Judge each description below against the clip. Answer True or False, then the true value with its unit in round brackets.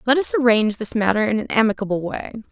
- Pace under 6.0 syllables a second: False (6.9 syllables/s)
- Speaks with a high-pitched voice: True (225 Hz)